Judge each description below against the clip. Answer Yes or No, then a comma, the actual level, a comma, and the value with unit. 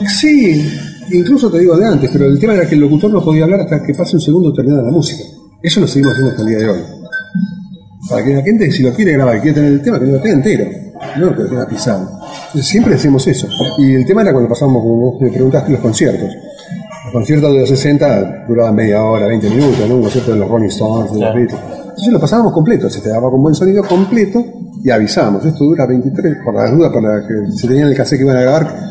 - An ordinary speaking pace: No, fast, 245 wpm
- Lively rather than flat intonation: Yes, wide, 6.0 semitones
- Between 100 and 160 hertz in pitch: Yes, medium, 140 Hz